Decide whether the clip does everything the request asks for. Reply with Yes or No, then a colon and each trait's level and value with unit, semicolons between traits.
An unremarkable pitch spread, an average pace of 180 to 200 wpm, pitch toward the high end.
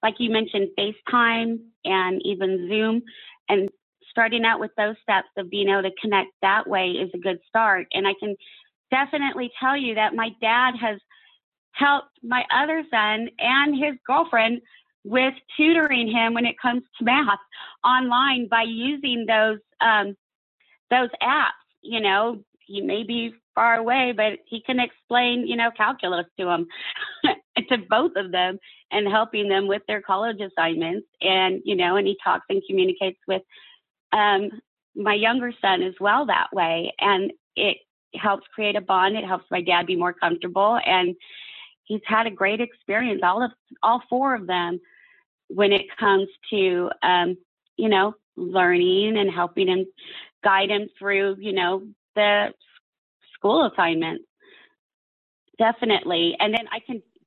No: average, 4.1 semitones; average, 155 wpm; high, 215 Hz